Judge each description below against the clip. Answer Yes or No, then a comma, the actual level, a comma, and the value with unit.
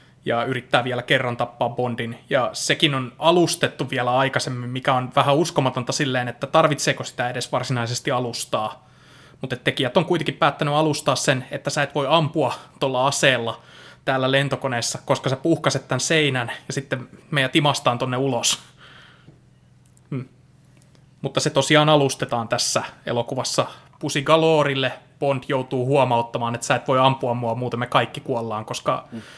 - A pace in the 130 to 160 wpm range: Yes, average, 150 wpm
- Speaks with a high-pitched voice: No, low, 135 Hz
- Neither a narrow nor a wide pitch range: Yes, average, 3.0 semitones